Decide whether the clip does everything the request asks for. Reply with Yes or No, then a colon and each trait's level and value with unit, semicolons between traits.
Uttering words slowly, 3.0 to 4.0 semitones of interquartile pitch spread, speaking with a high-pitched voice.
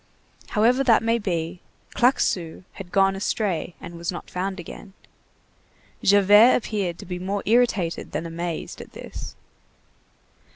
Yes: slow, 130 wpm; average, 3.6 semitones; high, 195 Hz